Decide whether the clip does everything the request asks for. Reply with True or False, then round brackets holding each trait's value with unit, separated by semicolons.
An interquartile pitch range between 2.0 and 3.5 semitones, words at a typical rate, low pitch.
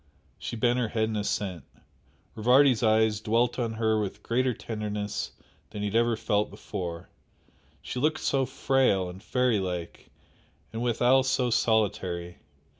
True (3.2 semitones; 145 wpm; 110 Hz)